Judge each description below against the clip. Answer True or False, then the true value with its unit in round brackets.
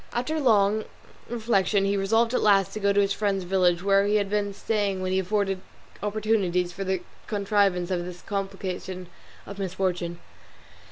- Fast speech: False (165 wpm)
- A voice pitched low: False (195 Hz)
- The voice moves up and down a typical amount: False (1.9 semitones)